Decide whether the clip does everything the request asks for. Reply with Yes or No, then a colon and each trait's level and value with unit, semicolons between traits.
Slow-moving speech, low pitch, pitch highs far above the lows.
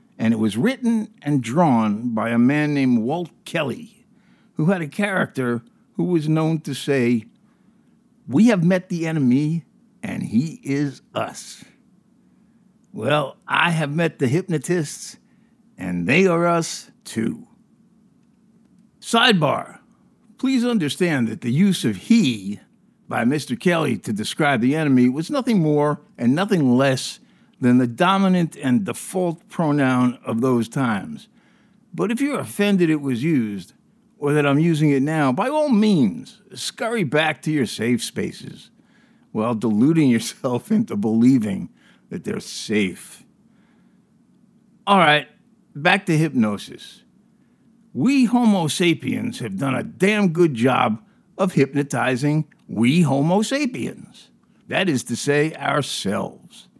No: slow, 130 wpm; medium, 175 Hz; wide, 7.9 semitones